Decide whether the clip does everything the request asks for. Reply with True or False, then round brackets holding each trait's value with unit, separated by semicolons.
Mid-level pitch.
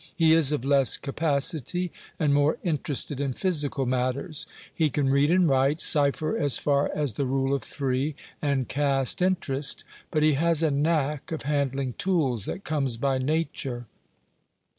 True (145 Hz)